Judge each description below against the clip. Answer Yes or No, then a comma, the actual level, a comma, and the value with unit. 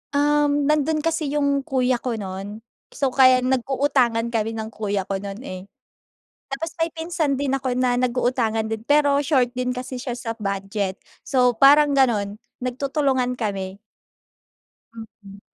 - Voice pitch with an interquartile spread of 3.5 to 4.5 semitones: Yes, average, 4.1 semitones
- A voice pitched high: Yes, very high, 250 Hz